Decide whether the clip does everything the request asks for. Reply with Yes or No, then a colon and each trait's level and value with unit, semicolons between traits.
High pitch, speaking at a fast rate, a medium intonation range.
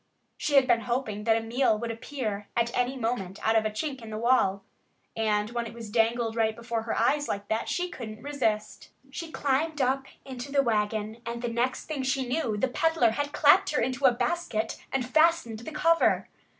Yes: high, 235 Hz; fast, 210 wpm; average, 3.5 semitones